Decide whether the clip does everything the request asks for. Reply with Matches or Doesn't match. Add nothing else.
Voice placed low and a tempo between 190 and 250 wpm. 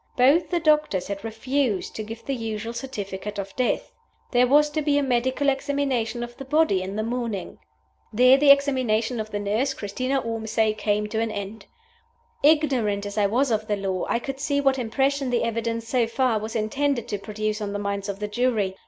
Doesn't match